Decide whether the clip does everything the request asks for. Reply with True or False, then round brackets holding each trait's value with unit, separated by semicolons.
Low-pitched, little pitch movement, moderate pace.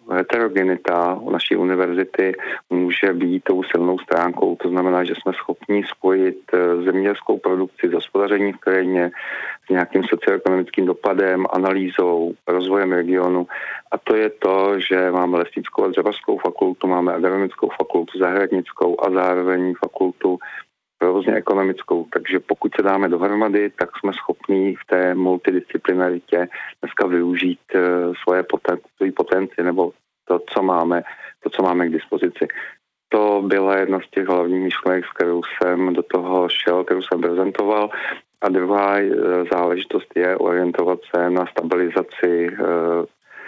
True (90 Hz; 1.1 semitones; 135 wpm)